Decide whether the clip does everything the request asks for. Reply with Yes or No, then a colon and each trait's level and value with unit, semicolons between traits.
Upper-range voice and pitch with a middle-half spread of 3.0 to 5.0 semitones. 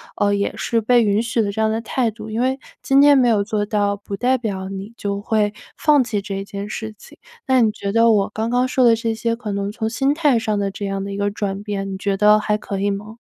No: high, 215 Hz; narrow, 2.4 semitones